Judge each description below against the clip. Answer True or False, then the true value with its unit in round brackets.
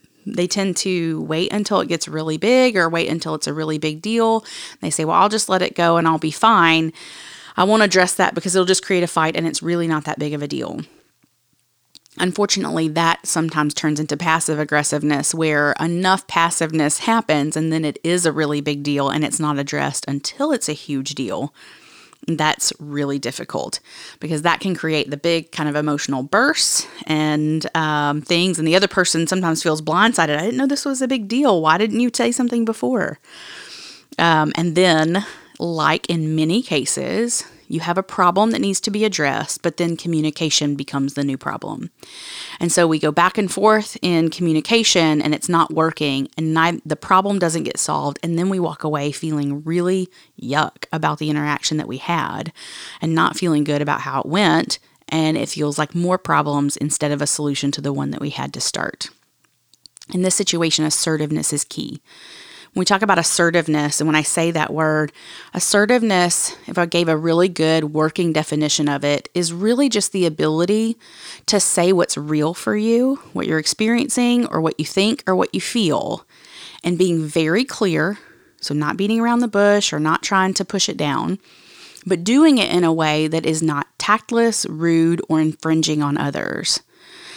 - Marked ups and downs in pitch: False (3.8 semitones)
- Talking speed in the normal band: True (190 wpm)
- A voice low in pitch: False (165 Hz)